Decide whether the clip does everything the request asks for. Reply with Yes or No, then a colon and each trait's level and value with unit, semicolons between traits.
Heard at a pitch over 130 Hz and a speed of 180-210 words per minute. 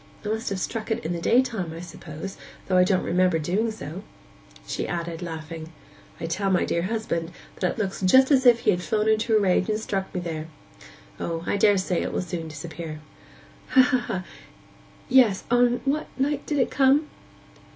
Yes: high, 190 Hz; average, 190 wpm